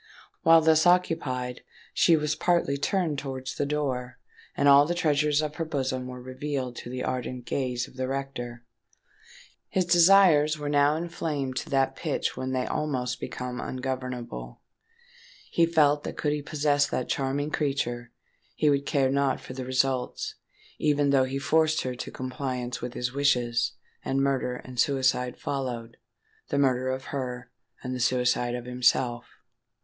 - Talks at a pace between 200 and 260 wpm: No, average, 155 wpm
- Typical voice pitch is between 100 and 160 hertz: Yes, low, 135 Hz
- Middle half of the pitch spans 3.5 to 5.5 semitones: No, average, 2.7 semitones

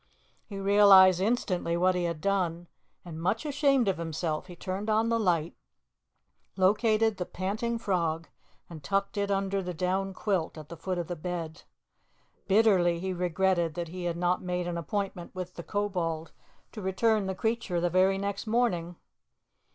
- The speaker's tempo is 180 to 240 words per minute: No, average, 165 wpm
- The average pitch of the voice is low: No, medium, 185 Hz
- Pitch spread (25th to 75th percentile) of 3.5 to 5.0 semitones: No, average, 2.8 semitones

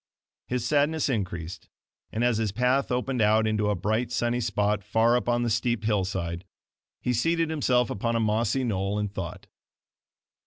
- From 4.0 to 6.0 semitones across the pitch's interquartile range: No, average, 3.1 semitones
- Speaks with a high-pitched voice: No, low, 115 Hz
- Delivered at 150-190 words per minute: Yes, average, 165 wpm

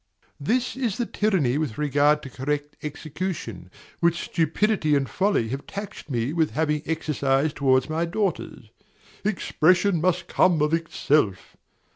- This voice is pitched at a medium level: Yes, medium, 155 Hz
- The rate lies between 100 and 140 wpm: Yes, slow, 135 wpm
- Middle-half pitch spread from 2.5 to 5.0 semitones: Yes, average, 4.5 semitones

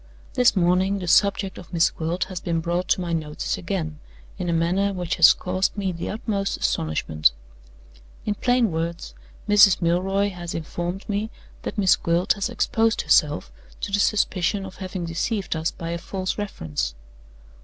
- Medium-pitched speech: Yes, medium, 180 Hz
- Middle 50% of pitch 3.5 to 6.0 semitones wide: No, average, 3.0 semitones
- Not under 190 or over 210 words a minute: No, average, 165 wpm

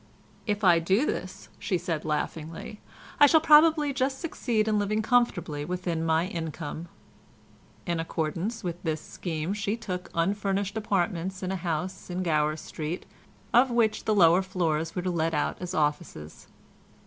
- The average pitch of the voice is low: No, medium, 180 Hz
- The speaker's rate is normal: Yes, average, 150 wpm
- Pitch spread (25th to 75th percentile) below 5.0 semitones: Yes, average, 4.4 semitones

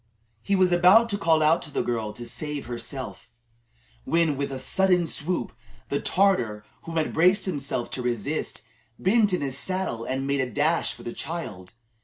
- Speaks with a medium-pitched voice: Yes, medium, 150 Hz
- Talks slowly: No, average, 185 wpm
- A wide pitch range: Yes, wide, 6.3 semitones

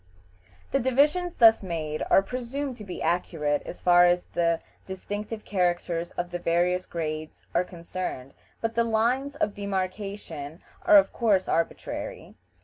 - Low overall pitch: No, medium, 185 Hz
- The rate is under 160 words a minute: Yes, average, 140 wpm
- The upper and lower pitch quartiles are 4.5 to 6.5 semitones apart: Yes, average, 5.1 semitones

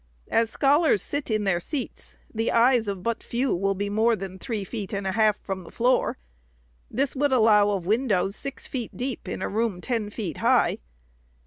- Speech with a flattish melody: No, average, 3.9 semitones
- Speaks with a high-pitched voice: Yes, high, 220 Hz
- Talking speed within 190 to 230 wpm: Yes, average, 195 wpm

